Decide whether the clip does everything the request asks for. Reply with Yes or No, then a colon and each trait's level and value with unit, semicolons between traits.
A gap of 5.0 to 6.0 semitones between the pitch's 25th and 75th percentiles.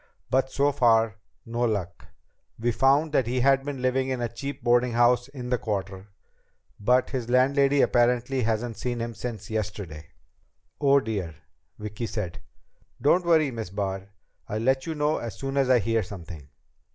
No: average, 3.7 semitones